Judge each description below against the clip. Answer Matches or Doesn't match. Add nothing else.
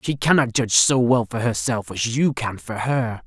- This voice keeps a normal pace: Doesn't match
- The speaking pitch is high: Doesn't match